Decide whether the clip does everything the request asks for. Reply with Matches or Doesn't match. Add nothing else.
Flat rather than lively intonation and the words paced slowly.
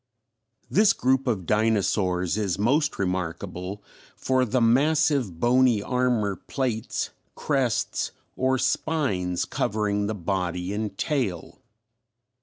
Doesn't match